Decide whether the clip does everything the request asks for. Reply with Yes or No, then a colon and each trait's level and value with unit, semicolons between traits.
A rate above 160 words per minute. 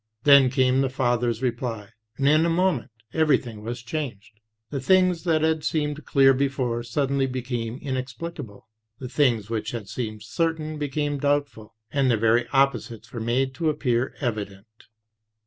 No: average, 150 wpm